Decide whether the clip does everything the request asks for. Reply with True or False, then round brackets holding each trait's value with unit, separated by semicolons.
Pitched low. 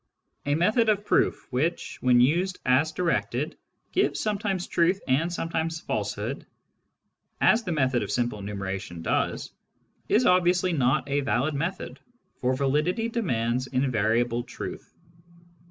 False (150 Hz)